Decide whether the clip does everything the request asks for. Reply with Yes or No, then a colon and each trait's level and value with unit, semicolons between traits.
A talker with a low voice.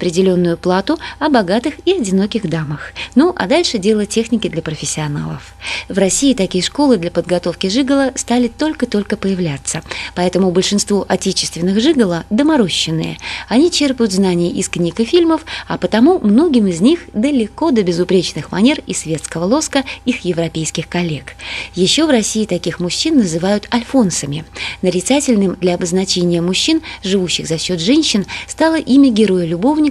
No: high, 195 Hz